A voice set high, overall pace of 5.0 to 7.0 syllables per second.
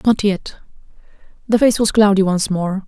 No: high, 200 Hz; 4.8 syllables/s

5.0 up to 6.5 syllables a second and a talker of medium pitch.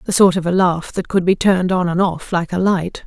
Yes: 5.5 syllables/s; medium, 180 Hz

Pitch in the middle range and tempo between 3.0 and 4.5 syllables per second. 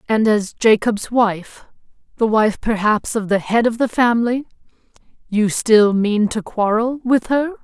No: high, 225 Hz; 4.2 syllables/s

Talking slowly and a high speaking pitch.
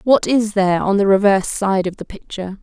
No: fast, 230 wpm; high, 200 Hz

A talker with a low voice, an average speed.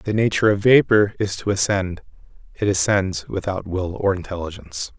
Yes: low, 100 Hz; average, 155 wpm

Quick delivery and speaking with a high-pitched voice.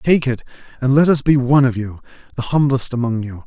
No: fast, 225 wpm; low, 130 Hz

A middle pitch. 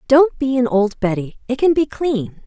No: very high, 250 Hz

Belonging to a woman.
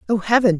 Yes: female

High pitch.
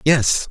No: medium, 140 Hz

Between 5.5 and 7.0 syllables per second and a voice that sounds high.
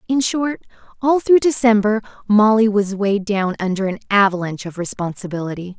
Yes: 5.6 syllables/s; high, 210 Hz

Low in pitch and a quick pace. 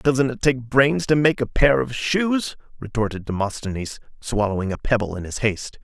No: low, 120 Hz; average, 185 wpm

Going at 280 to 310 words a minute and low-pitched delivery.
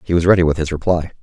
Yes: fast, 295 wpm; very low, 85 Hz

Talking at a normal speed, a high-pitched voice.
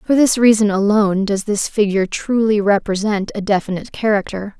Yes: average, 155 wpm; high, 205 Hz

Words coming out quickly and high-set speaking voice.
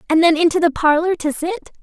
Yes: fast, 230 wpm; very high, 330 Hz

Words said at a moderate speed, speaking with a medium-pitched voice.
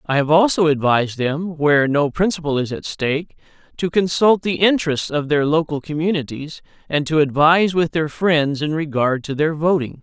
Yes: average, 180 wpm; medium, 155 Hz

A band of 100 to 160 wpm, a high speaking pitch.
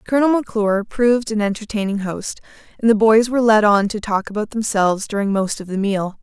No: average, 200 wpm; high, 210 Hz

